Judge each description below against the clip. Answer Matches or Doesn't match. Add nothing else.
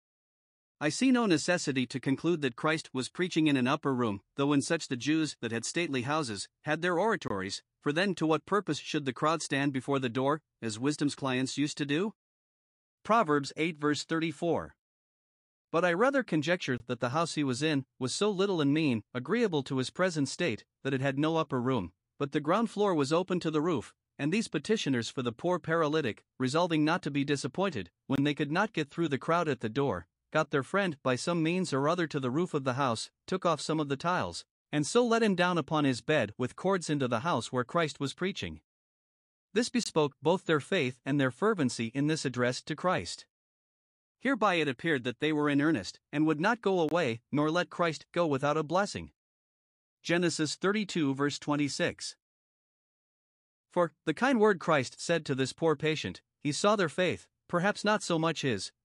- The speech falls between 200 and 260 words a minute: Matches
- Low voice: Doesn't match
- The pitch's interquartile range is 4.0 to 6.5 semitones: Matches